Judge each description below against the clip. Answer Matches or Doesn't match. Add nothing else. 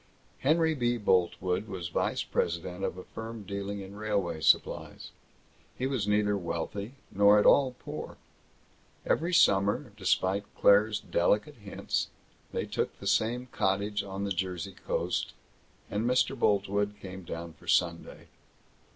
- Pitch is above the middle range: Doesn't match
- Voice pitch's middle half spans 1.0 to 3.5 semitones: Matches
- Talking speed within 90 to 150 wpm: Matches